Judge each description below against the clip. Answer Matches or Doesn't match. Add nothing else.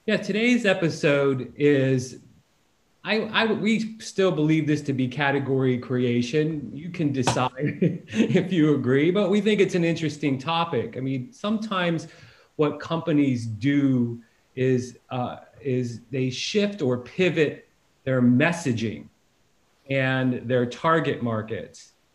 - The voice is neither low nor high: Matches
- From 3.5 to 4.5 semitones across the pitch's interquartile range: Doesn't match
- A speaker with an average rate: Doesn't match